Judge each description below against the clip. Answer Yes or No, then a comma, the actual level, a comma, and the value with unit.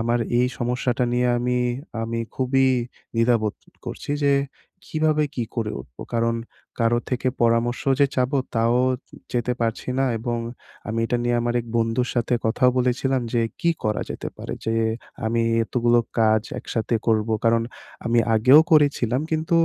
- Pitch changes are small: Yes, narrow, 1.7 semitones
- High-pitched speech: No, low, 120 Hz